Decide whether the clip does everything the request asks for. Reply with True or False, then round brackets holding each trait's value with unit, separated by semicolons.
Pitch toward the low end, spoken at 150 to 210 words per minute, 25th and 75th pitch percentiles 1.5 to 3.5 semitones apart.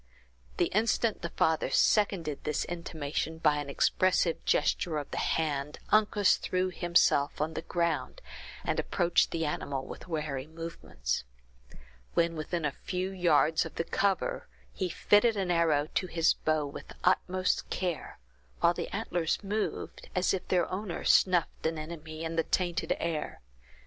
False (170 Hz; 155 wpm; 2.9 semitones)